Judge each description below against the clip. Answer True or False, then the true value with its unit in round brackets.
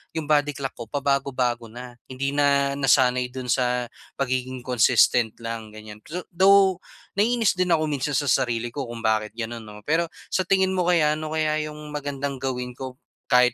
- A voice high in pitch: False (135 Hz)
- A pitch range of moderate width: True (3.6 semitones)